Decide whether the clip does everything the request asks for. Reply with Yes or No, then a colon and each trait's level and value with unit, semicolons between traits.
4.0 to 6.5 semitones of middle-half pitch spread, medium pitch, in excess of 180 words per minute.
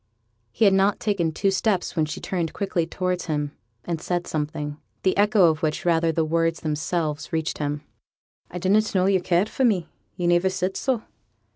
No: average, 3.2 semitones; medium, 175 Hz; average, 190 wpm